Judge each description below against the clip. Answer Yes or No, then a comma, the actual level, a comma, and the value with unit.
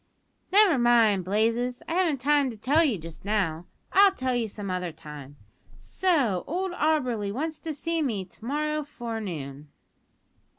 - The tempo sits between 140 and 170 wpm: Yes, average, 155 wpm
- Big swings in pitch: Yes, wide, 7.8 semitones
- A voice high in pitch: Yes, high, 240 Hz